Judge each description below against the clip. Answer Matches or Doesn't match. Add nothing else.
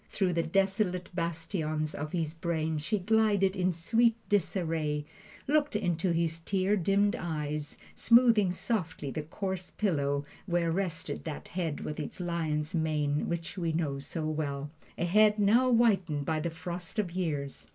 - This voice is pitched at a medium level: Matches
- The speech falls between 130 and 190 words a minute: Matches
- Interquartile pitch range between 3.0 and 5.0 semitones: Matches